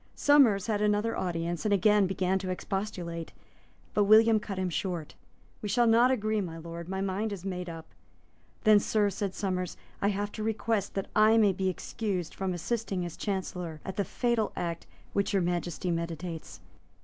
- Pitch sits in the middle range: No, high, 195 Hz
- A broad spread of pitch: No, average, 3.1 semitones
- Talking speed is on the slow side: No, average, 175 wpm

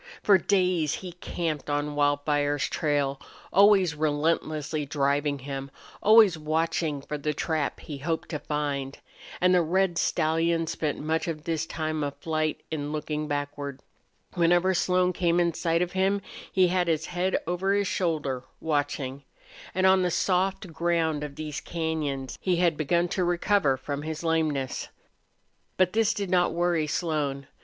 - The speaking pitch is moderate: Yes, medium, 160 Hz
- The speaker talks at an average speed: Yes, average, 155 wpm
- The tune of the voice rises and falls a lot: No, average, 3.3 semitones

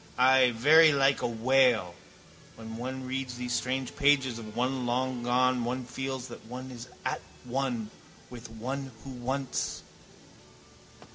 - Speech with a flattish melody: Yes, narrow, 1.6 semitones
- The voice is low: Yes, low, 125 Hz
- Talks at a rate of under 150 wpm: Yes, average, 140 wpm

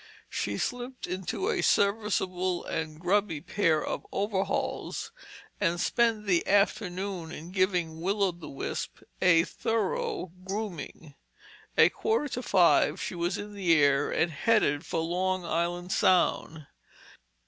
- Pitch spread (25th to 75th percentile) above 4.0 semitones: No, average, 3.6 semitones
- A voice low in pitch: No, medium, 185 Hz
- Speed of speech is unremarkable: No, slow, 130 wpm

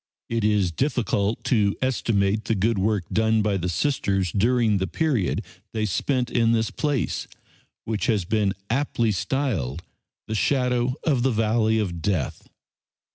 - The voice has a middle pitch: No, low, 110 Hz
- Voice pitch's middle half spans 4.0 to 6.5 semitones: No, average, 3.6 semitones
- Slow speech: No, average, 145 wpm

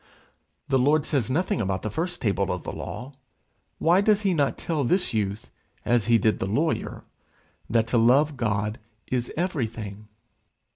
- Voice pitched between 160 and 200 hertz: No, low, 120 Hz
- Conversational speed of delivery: Yes, average, 160 wpm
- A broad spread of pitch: Yes, wide, 6.4 semitones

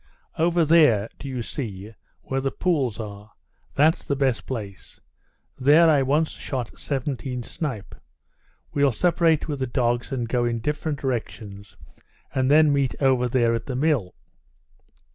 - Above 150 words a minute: No, average, 145 wpm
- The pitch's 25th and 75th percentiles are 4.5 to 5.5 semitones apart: No, average, 4.0 semitones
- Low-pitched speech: Yes, low, 130 Hz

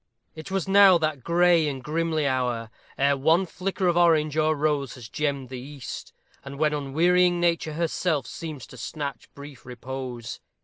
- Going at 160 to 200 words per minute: Yes, average, 165 wpm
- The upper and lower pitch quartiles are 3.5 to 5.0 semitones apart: Yes, average, 3.9 semitones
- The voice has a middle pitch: Yes, medium, 150 Hz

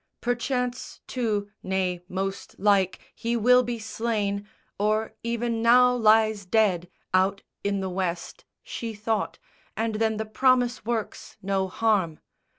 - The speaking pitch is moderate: No, high, 215 Hz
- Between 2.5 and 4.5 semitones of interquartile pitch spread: Yes, average, 3.1 semitones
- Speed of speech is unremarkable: No, slow, 130 wpm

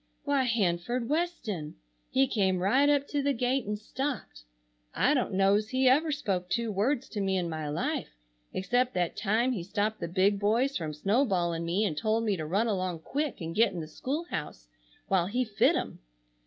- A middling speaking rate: Yes, average, 195 wpm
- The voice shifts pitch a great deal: Yes, wide, 6.1 semitones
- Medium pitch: No, high, 210 Hz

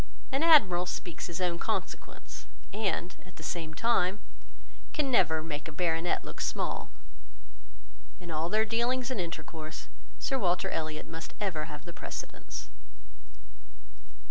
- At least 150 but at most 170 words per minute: No, slow, 135 wpm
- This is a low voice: No, medium, 175 Hz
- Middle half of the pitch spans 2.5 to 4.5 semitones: No, average, 4.9 semitones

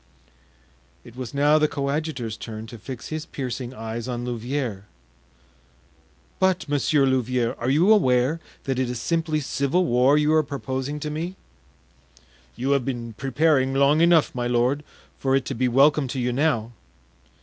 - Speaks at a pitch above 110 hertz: Yes, low, 135 Hz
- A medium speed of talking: Yes, average, 160 wpm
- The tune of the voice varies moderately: Yes, average, 3.6 semitones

